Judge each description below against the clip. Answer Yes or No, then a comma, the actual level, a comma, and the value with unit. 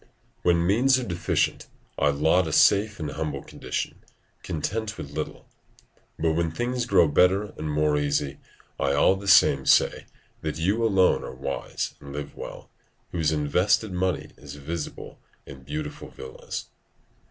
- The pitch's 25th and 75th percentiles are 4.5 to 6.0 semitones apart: Yes, average, 4.8 semitones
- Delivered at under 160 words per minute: Yes, average, 150 wpm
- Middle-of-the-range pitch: No, very low, 80 Hz